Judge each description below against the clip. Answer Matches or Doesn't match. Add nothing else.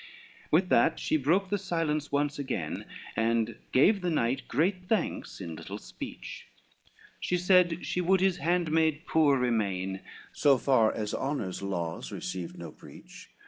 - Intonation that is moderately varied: Doesn't match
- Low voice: Doesn't match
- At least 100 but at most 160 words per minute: Matches